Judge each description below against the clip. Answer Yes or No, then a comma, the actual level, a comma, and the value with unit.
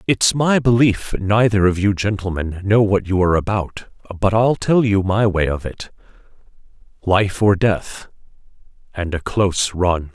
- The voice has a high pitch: No, low, 100 Hz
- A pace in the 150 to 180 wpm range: Yes, average, 155 wpm